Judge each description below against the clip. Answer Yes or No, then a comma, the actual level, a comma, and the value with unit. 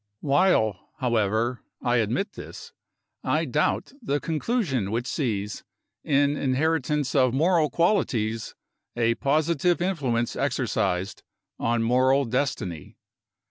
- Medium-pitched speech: No, low, 130 Hz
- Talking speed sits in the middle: No, slow, 100 wpm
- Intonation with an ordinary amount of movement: Yes, average, 5.0 semitones